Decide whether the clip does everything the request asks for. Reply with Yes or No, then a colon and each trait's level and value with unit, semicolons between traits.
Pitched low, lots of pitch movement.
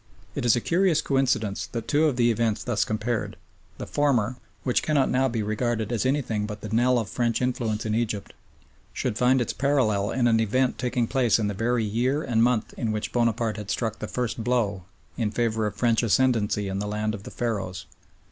No: low, 115 Hz; narrow, 2.6 semitones